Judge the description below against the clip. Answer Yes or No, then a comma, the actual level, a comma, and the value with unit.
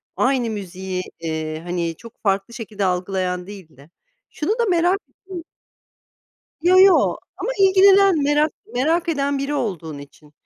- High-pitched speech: Yes, high, 225 Hz